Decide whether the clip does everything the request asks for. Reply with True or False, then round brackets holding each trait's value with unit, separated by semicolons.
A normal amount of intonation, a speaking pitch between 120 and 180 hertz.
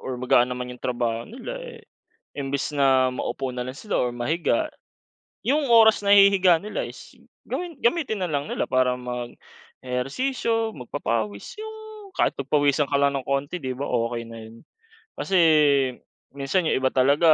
False (8.2 semitones; 140 Hz)